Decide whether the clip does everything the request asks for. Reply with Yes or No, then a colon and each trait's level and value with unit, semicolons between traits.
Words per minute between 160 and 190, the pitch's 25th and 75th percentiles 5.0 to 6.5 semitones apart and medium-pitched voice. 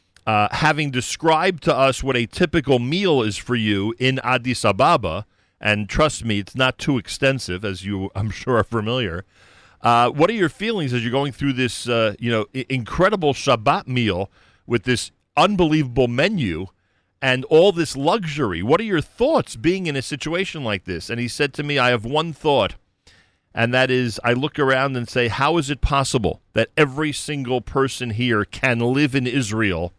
No: average, 185 wpm; wide, 5.6 semitones; low, 125 Hz